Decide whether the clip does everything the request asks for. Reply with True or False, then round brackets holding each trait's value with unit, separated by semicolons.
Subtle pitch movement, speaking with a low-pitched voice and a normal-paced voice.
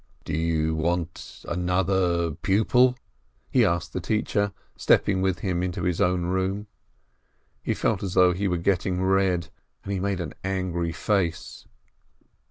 True (2.0 semitones; 90 Hz; 150 wpm)